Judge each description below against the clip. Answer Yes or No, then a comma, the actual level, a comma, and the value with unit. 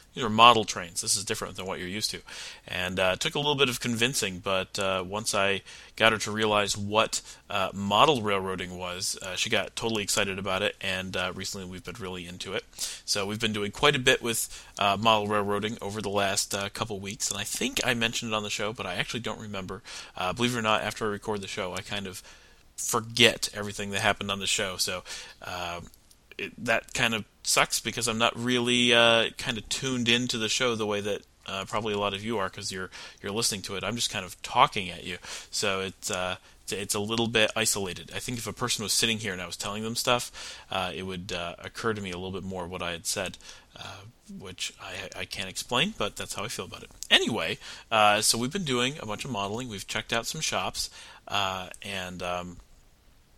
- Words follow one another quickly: Yes, fast, 235 wpm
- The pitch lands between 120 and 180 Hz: No, low, 105 Hz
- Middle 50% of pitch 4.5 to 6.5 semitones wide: No, average, 3.3 semitones